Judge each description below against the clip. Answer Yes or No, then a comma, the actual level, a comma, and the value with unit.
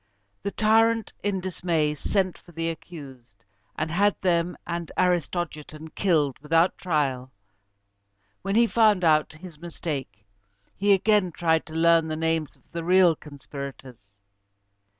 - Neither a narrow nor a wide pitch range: Yes, average, 3.5 semitones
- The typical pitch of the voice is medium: Yes, medium, 165 Hz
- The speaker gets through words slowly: Yes, slow, 130 wpm